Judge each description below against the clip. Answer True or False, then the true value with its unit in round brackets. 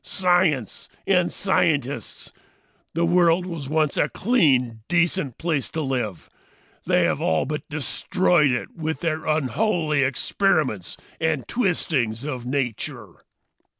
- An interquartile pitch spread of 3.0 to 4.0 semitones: False (4.9 semitones)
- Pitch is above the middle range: False (155 Hz)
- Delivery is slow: True (115 wpm)